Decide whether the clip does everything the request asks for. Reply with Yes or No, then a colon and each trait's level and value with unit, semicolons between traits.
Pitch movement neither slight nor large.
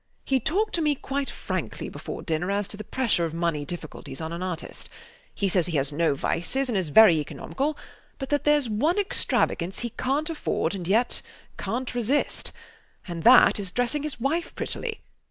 No: wide, 8.4 semitones